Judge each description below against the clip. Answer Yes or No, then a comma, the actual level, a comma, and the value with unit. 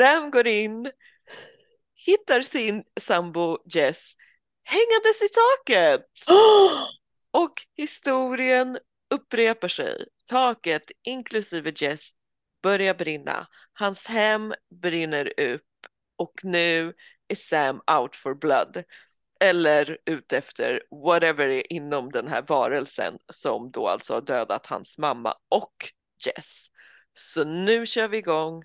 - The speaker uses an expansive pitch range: Yes, wide, 7.7 semitones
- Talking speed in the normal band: No, slow, 115 wpm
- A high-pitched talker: Yes, high, 215 Hz